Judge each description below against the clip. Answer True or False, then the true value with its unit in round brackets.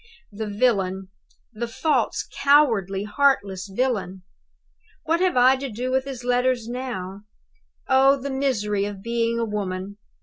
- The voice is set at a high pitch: True (235 Hz)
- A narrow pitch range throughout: False (4.7 semitones)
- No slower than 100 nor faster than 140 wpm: True (135 wpm)